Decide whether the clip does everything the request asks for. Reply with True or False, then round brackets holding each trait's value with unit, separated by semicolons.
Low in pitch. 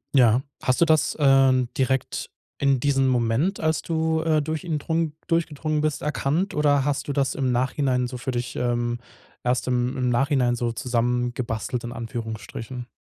True (130 Hz)